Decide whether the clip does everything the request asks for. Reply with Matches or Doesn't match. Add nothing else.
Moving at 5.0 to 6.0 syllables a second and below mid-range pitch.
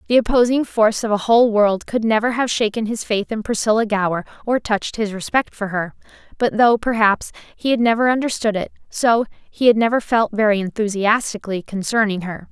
Doesn't match